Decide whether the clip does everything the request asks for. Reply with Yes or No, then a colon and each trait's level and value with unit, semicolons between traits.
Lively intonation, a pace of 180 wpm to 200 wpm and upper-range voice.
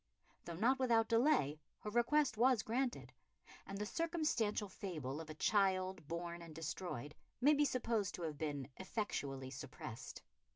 No: wide, 7.4 semitones; average, 150 wpm; high, 195 Hz